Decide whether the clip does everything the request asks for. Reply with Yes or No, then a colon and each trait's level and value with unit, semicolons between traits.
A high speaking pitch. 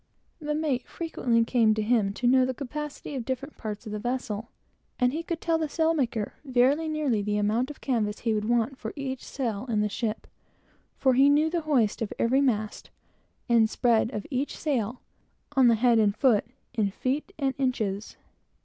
Yes: very high, 250 Hz